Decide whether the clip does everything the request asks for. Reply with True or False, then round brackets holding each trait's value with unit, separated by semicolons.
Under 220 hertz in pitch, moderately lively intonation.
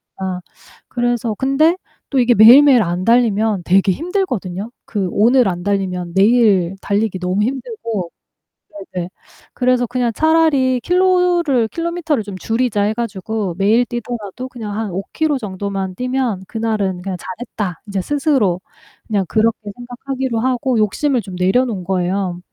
False (225 Hz; 4.8 semitones)